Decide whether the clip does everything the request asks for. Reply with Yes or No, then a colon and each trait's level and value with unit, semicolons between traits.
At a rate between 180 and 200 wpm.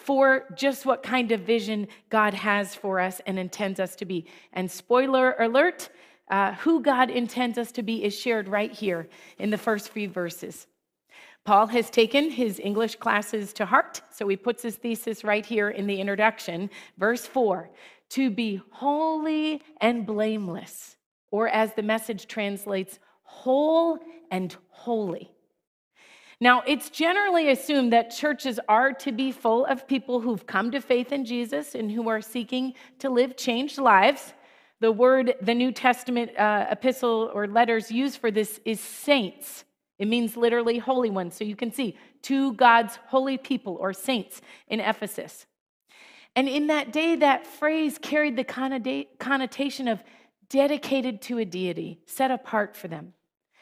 No: average, 160 wpm